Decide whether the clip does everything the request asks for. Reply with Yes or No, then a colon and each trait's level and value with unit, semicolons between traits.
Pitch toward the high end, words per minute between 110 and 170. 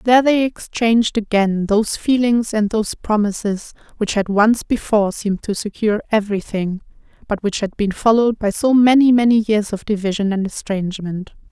Yes: high, 215 Hz; average, 160 wpm